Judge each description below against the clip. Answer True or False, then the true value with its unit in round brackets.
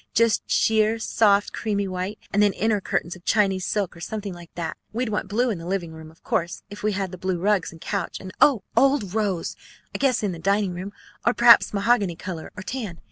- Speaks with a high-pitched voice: True (200 Hz)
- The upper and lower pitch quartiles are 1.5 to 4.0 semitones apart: True (3.1 semitones)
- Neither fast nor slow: False (225 wpm)